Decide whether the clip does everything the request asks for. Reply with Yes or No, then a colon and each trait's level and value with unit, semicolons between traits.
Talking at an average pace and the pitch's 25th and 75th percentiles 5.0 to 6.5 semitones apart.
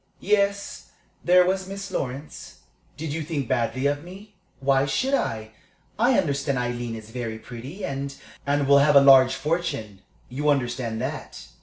Yes: average, 160 wpm; wide, 5.5 semitones